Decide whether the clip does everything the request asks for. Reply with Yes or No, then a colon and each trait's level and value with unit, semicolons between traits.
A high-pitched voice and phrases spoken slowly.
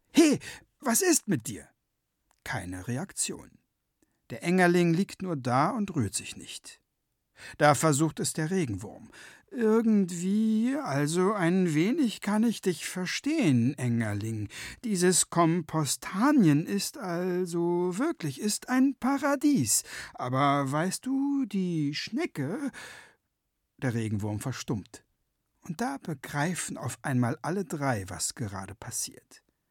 No: medium, 170 Hz; slow, 115 wpm